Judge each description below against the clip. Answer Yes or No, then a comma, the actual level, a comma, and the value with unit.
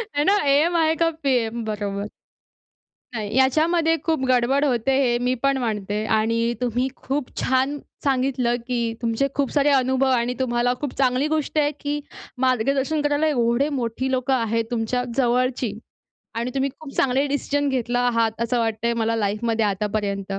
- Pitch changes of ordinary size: Yes, average, 3.3 semitones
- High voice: Yes, very high, 250 Hz